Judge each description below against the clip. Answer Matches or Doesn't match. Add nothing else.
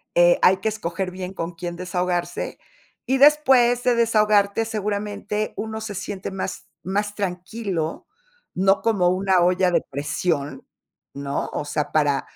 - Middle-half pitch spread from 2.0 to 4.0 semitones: Matches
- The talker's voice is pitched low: Doesn't match